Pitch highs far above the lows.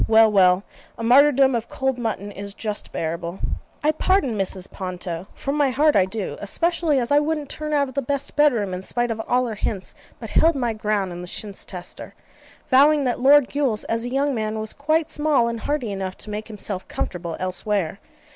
Yes: wide, 6.2 semitones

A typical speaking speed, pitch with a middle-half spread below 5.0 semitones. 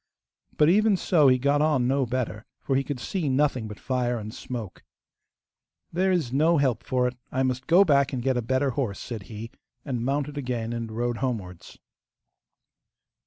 Yes: average, 180 wpm; average, 3.3 semitones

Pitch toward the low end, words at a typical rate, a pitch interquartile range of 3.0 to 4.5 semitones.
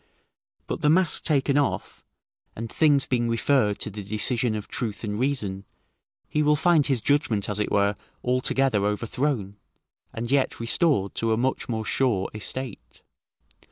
No: low, 120 Hz; average, 155 wpm; average, 5.0 semitones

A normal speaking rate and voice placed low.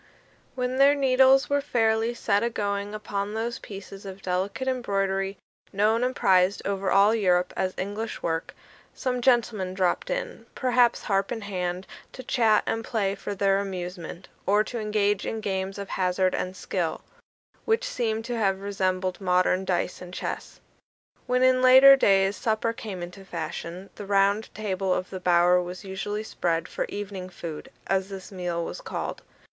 No: average, 165 wpm; high, 200 Hz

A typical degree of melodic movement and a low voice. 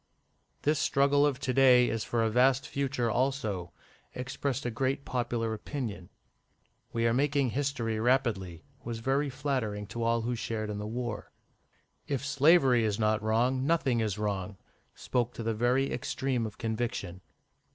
Yes: average, 3.5 semitones; low, 120 Hz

